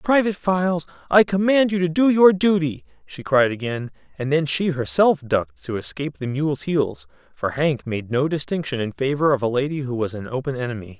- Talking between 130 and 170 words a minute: No, average, 195 wpm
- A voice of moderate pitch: Yes, medium, 145 Hz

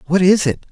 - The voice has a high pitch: No, medium, 175 Hz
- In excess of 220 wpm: Yes, fast, 250 wpm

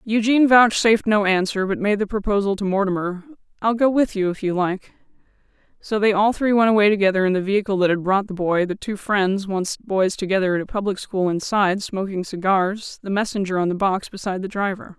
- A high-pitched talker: Yes, high, 200 Hz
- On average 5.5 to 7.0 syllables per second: No, 5.3 syllables/s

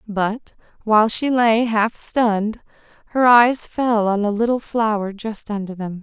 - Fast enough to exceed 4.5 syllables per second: No, 4.1 syllables/s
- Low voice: No, high, 220 Hz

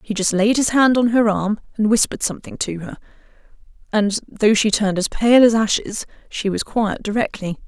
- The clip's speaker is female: Yes, female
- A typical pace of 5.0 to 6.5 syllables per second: Yes, 5.3 syllables/s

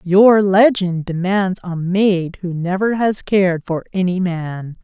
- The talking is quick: No, average, 150 wpm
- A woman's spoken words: Yes, female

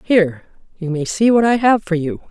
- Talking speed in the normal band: No, fast, 235 wpm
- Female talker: Yes, female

